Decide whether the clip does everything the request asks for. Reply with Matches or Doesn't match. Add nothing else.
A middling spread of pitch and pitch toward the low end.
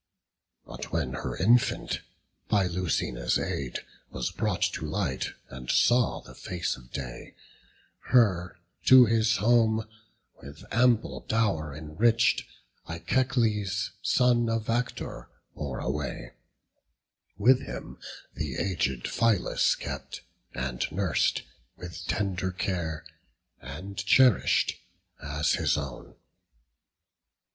Doesn't match